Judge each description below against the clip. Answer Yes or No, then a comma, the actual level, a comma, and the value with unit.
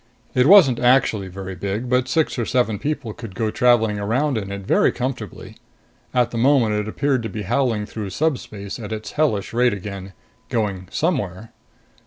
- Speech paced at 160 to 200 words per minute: Yes, average, 175 wpm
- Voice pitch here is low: Yes, low, 115 Hz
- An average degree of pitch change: Yes, average, 4.0 semitones